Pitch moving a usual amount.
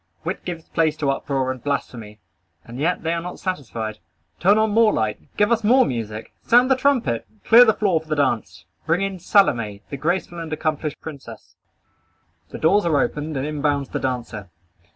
No: wide, 6.7 semitones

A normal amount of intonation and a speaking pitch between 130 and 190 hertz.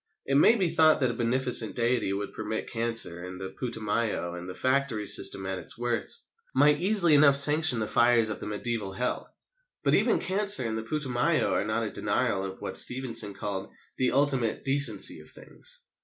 No: average, 4.9 semitones; low, 120 Hz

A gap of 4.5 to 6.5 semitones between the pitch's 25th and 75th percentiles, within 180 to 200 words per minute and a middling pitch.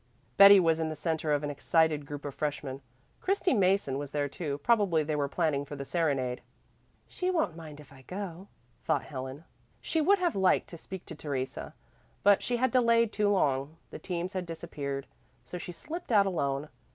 Yes: wide, 5.6 semitones; average, 190 wpm; medium, 160 Hz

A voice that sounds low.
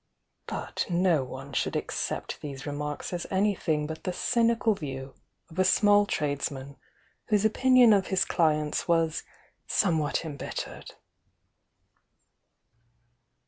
No: medium, 165 Hz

